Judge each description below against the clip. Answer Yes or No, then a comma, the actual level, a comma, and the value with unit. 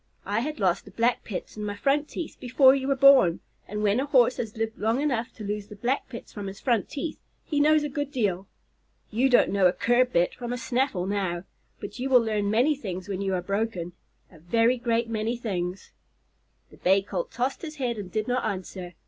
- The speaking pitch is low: No, high, 225 Hz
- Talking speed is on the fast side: Yes, fast, 225 wpm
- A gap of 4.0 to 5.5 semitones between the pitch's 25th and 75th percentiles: Yes, average, 4.6 semitones